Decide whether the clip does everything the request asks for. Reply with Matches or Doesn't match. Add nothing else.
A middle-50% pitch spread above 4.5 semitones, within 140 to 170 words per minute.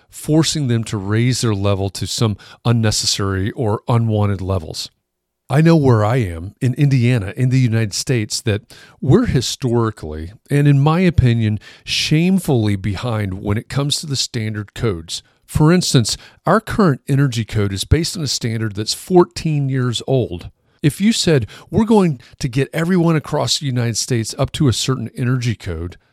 Matches